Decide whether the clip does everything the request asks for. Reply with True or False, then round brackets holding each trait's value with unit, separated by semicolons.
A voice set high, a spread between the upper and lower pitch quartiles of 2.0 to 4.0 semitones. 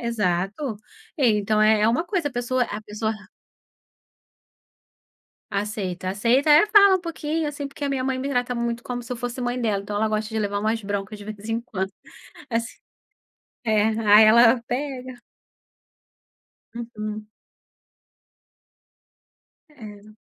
True (230 Hz; 3.3 semitones)